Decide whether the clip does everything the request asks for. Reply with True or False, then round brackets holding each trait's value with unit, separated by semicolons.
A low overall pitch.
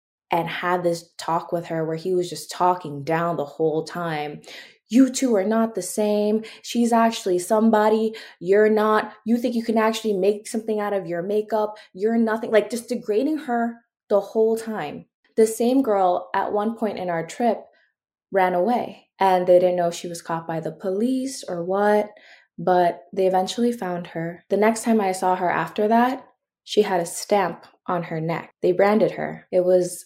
False (200 Hz)